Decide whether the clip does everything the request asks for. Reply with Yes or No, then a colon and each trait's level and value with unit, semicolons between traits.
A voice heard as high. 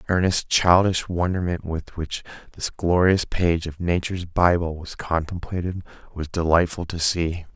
No: very low, 85 Hz